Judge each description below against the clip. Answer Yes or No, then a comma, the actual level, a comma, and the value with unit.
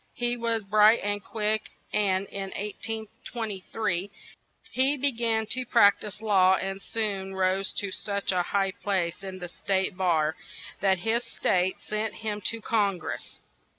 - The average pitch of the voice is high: Yes, high, 205 Hz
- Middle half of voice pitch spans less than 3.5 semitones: Yes, average, 2.7 semitones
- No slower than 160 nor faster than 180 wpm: No, average, 150 wpm